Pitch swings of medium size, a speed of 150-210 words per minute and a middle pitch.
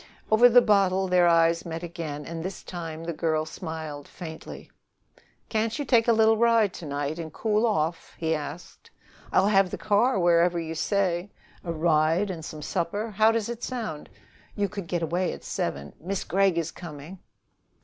Yes: average, 4.2 semitones; average, 175 wpm; medium, 175 Hz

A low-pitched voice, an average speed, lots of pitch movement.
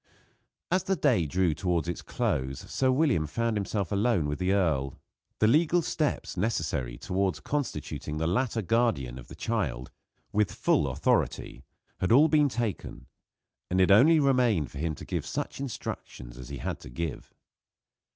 Yes: very low, 95 Hz; average, 160 wpm; wide, 8.6 semitones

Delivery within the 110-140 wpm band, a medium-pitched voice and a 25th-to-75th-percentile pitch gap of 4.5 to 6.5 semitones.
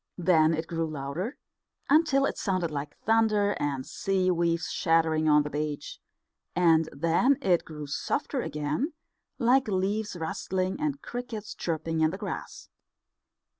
Yes: slow, 135 wpm; medium, 170 Hz; wide, 5.4 semitones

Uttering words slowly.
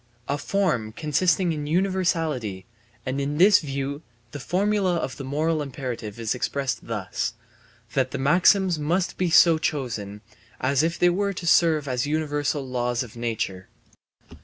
No: average, 150 wpm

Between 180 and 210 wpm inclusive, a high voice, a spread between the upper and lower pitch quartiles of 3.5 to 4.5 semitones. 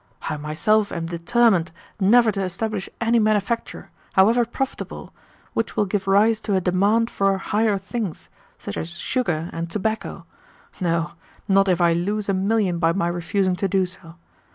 No: average, 160 wpm; high, 195 Hz; average, 3.8 semitones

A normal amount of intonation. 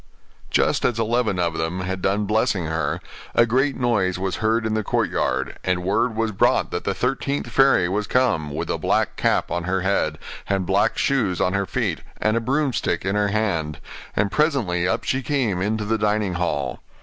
Yes: average, 4.0 semitones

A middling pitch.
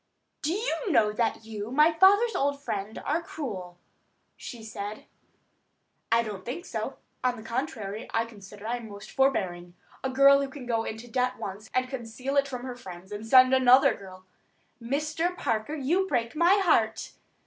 No: high, 245 Hz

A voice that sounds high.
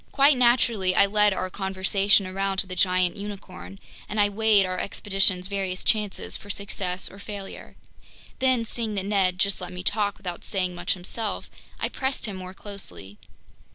Yes: high, 195 Hz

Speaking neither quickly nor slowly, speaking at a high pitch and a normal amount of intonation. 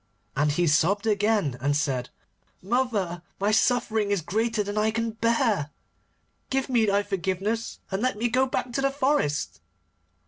Yes: average, 160 wpm; high, 210 Hz; average, 4.8 semitones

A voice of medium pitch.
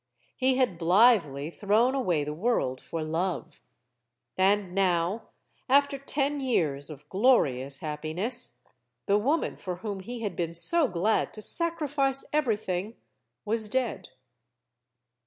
No: high, 205 Hz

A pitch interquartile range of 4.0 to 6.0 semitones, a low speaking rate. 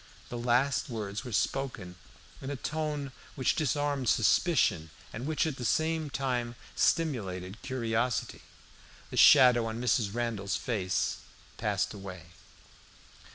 Yes: average, 4.6 semitones; slow, 120 wpm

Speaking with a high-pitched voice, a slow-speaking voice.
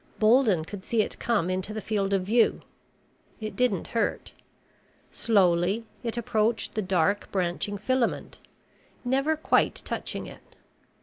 Yes: high, 215 Hz; slow, 130 wpm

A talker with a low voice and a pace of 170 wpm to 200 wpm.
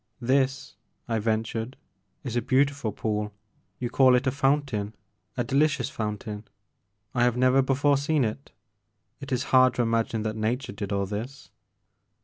No: low, 125 Hz; average, 160 wpm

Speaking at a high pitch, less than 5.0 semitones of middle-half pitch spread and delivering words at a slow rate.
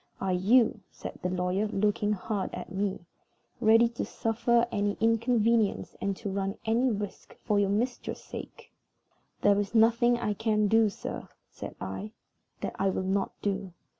No: high, 210 Hz; narrow, 2.5 semitones; average, 160 wpm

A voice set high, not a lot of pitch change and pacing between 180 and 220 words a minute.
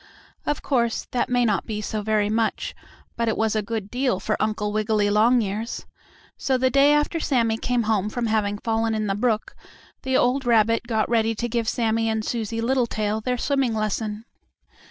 Yes: high, 225 Hz; narrow, 2.2 semitones; average, 185 wpm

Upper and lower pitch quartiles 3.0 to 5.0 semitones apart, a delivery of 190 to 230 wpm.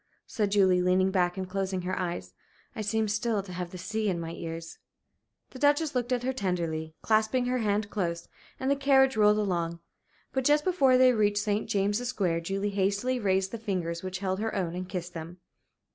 Yes: average, 3.9 semitones; average, 200 wpm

